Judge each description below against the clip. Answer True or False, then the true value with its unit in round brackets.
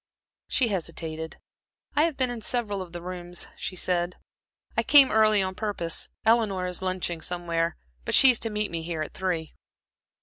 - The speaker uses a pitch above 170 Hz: True (185 Hz)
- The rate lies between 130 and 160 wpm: False (175 wpm)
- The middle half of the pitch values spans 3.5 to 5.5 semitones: True (4.1 semitones)